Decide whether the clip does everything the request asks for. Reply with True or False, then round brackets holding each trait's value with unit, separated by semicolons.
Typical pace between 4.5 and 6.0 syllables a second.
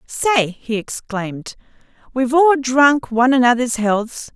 False (4.1 syllables/s)